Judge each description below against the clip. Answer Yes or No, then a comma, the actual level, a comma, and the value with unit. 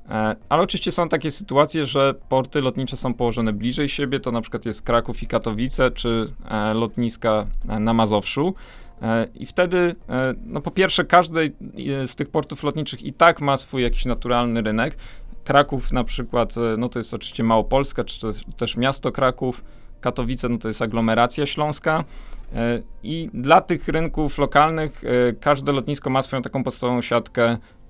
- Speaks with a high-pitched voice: No, low, 125 Hz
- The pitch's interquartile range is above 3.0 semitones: Yes, average, 3.8 semitones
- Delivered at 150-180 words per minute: Yes, average, 155 wpm